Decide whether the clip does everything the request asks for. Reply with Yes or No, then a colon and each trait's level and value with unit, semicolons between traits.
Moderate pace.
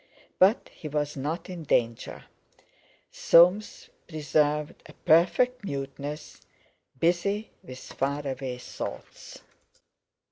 No: slow, 95 wpm